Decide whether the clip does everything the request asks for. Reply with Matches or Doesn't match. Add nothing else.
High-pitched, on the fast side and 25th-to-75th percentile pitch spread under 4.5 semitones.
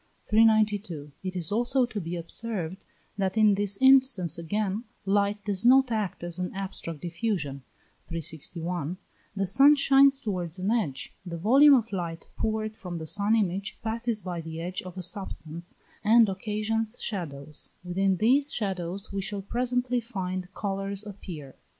Doesn't match